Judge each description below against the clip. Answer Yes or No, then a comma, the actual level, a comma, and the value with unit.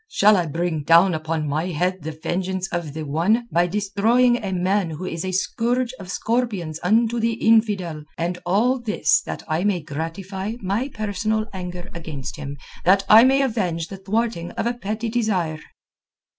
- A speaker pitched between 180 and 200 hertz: Yes, high, 190 Hz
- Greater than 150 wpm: Yes, average, 170 wpm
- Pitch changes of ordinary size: Yes, average, 4.7 semitones